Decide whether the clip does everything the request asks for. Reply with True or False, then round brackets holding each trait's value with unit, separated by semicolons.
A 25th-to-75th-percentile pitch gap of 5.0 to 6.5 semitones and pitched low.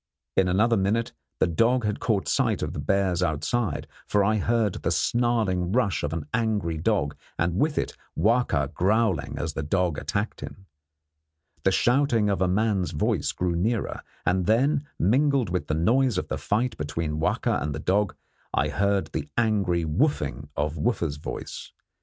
True (5.3 semitones; 95 Hz)